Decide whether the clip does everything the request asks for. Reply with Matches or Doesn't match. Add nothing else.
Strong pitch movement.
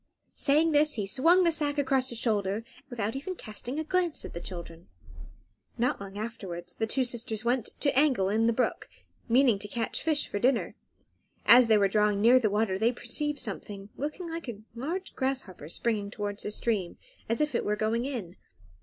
Doesn't match